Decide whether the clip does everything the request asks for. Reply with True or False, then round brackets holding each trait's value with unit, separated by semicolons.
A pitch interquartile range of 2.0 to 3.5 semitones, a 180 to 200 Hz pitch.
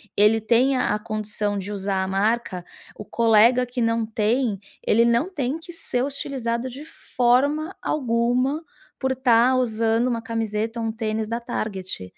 False (2.8 semitones; 230 Hz)